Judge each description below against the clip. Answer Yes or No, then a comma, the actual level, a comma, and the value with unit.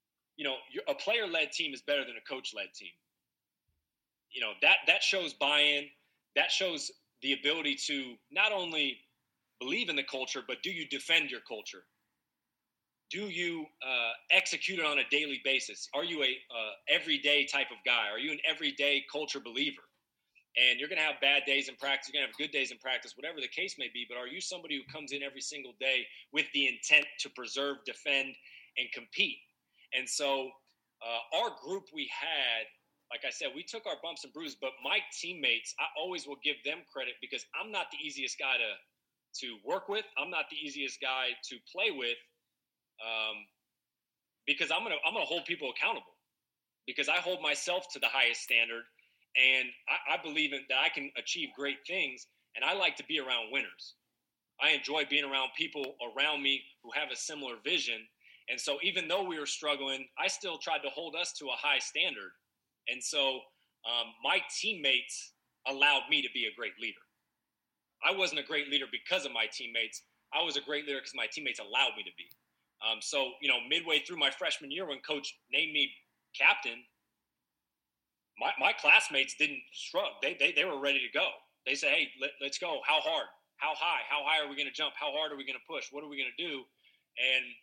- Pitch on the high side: No, medium, 140 Hz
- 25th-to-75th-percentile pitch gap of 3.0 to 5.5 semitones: No, narrow, 2.6 semitones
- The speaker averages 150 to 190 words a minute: No, average, 200 wpm